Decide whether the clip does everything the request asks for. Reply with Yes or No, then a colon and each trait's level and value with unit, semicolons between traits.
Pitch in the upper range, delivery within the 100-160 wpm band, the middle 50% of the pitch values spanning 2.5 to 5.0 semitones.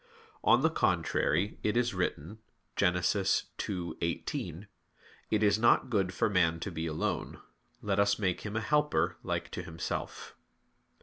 No: low, 100 Hz; average, 140 wpm; average, 4.0 semitones